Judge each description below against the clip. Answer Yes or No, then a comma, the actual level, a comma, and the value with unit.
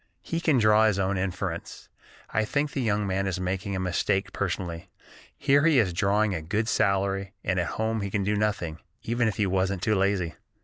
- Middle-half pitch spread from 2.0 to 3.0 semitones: Yes, narrow, 2.5 semitones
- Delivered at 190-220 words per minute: Yes, fast, 205 wpm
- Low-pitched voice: Yes, low, 100 Hz